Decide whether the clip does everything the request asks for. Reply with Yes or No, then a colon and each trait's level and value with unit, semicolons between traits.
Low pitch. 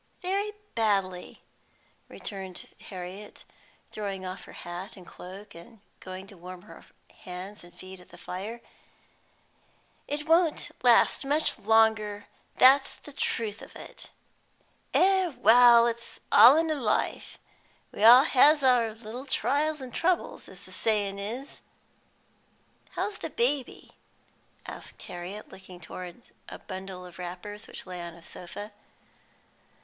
No: high, 215 Hz